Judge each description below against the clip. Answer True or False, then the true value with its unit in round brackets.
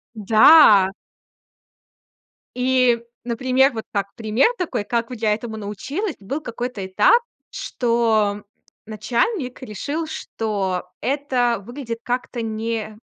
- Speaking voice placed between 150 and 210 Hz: False (230 Hz)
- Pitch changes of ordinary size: True (3.2 semitones)